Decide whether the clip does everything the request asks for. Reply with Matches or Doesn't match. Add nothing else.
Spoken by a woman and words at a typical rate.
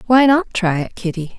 Doesn't match